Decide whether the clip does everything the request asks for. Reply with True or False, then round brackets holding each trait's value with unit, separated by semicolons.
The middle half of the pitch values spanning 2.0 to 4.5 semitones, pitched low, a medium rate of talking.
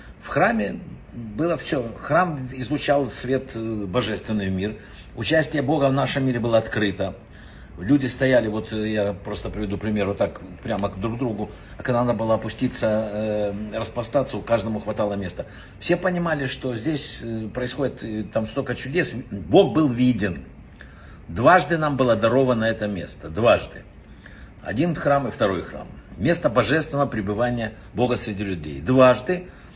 True (4.2 semitones; 115 Hz; 140 wpm)